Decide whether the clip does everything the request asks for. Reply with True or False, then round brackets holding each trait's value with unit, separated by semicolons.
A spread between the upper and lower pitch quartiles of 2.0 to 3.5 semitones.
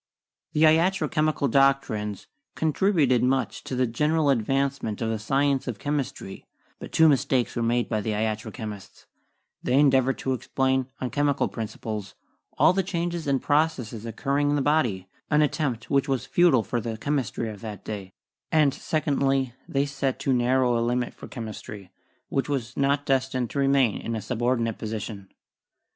False (3.9 semitones)